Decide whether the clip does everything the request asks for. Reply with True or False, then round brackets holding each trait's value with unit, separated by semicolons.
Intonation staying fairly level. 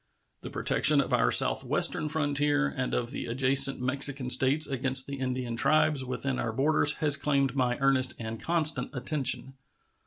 True (2.2 semitones)